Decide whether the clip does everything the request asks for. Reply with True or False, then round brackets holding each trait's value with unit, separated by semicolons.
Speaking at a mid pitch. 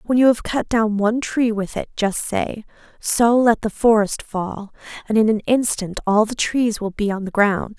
False (220 Hz)